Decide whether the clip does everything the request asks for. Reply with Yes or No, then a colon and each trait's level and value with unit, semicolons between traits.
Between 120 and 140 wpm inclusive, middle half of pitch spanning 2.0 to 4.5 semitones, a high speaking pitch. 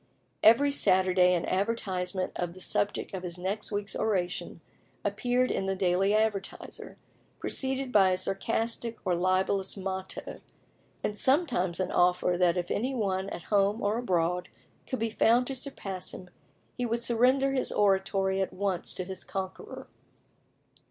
No: average, 150 wpm; average, 3.7 semitones; high, 195 Hz